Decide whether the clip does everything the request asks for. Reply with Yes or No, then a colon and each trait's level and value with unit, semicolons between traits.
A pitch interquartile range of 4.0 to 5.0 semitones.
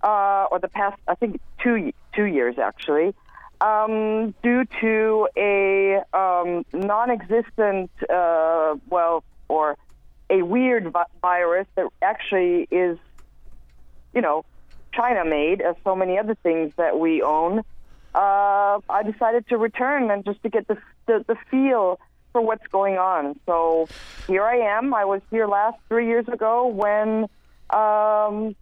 Yes: average, 4.4 semitones